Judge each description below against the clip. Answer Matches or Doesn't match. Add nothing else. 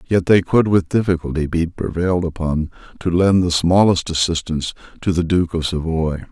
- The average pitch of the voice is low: Matches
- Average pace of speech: Matches